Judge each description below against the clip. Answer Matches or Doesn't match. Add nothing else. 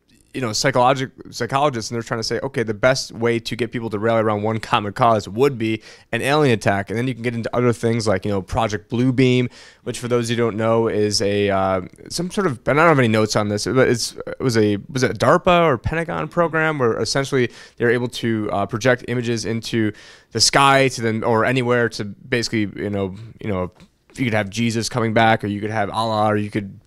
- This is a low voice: Matches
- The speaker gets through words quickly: Matches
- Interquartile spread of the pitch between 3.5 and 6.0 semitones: Doesn't match